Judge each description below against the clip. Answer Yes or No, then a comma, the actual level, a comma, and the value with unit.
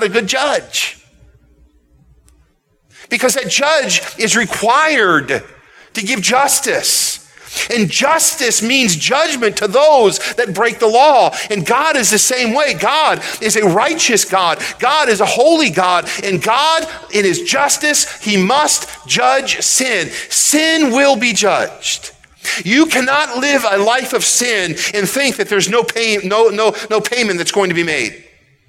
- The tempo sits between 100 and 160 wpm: Yes, average, 150 wpm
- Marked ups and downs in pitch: Yes, wide, 5.7 semitones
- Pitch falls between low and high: No, high, 230 Hz